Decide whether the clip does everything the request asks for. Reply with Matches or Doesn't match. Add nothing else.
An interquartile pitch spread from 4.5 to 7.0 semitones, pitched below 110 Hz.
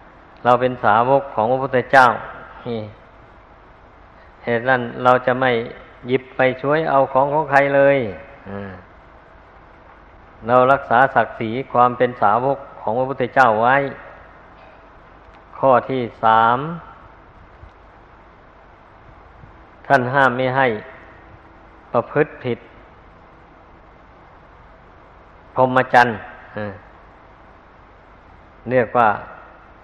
Doesn't match